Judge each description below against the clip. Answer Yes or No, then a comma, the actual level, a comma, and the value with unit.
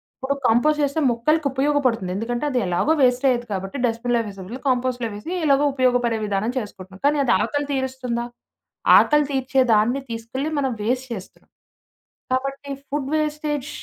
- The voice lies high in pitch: Yes, very high, 255 Hz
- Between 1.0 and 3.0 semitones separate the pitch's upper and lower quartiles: No, average, 3.4 semitones